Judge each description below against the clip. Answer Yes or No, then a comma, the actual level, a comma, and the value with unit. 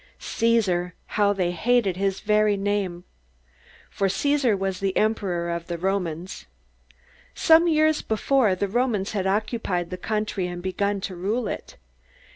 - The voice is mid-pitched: No, high, 200 Hz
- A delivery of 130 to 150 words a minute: Yes, average, 140 wpm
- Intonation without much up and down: No, average, 3.2 semitones